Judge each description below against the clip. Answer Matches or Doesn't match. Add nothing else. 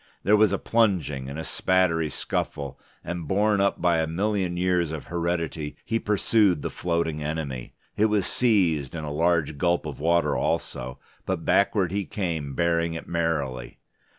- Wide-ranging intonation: Doesn't match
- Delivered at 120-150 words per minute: Doesn't match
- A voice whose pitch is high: Doesn't match